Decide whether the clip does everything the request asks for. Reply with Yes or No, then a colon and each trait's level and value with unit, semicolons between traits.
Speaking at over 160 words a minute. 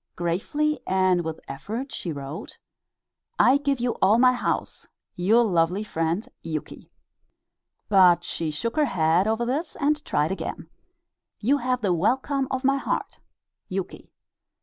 No: average, 140 wpm